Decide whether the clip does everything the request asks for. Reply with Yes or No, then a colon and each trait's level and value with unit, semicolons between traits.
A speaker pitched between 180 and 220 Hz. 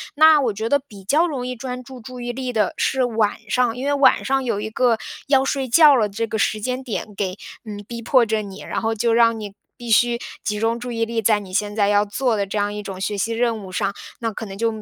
No: high, 230 Hz